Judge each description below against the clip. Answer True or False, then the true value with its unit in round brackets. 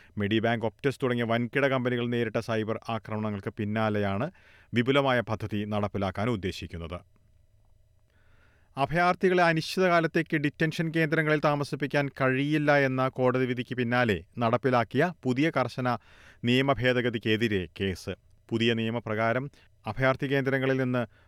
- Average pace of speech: True (95 wpm)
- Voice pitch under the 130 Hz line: True (120 Hz)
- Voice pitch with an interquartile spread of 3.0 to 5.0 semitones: True (4.5 semitones)